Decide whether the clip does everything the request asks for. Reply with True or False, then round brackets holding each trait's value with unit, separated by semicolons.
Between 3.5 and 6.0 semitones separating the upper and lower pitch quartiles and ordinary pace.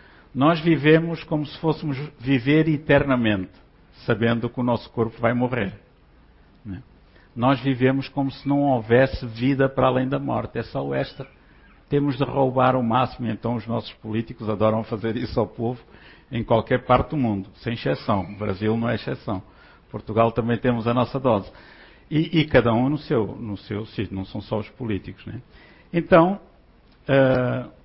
True (3.9 semitones; 170 wpm)